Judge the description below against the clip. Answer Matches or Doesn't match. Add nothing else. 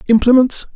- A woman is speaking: Doesn't match